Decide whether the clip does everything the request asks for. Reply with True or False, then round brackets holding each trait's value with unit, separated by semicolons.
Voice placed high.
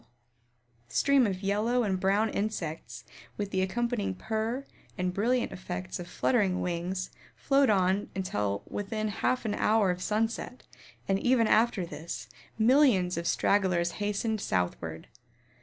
True (200 Hz)